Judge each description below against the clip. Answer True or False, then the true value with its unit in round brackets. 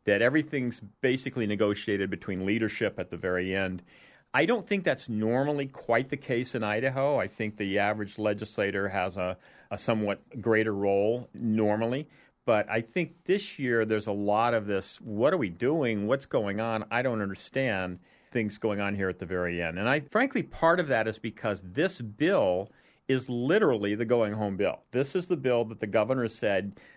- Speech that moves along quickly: False (185 wpm)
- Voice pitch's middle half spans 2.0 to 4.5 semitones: True (3.9 semitones)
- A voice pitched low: True (110 Hz)